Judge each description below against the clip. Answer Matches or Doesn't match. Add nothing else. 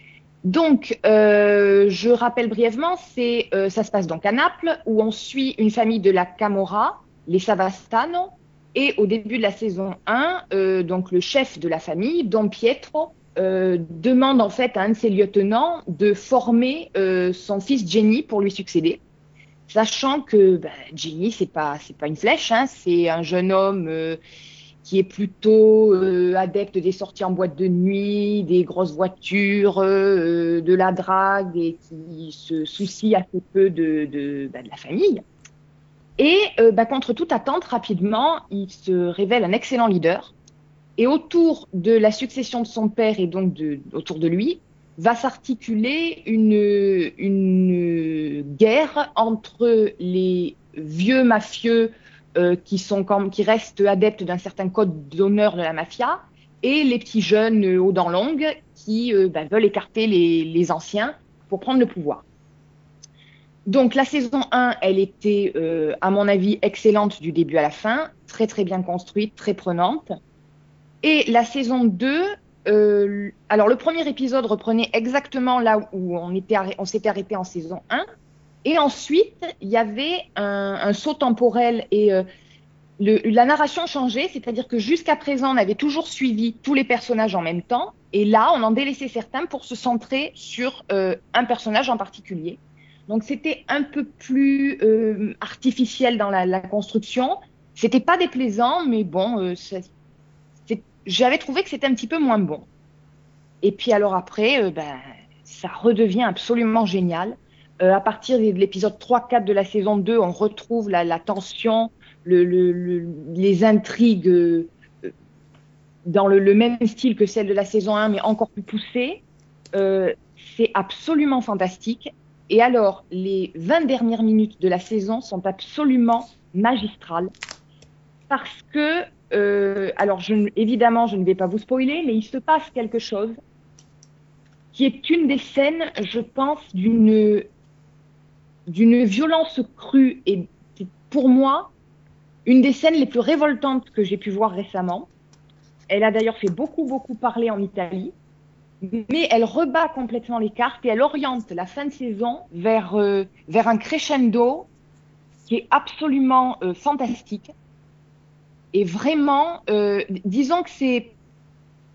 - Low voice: Doesn't match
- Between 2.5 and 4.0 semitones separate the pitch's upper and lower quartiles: Doesn't match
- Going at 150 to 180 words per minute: Matches